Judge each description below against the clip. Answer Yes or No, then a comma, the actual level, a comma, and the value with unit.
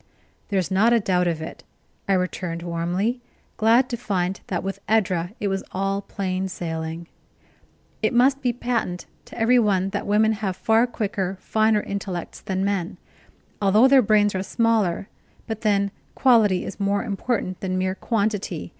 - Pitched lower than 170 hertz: No, high, 200 Hz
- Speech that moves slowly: No, average, 160 wpm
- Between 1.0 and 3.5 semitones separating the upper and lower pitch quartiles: Yes, average, 3.1 semitones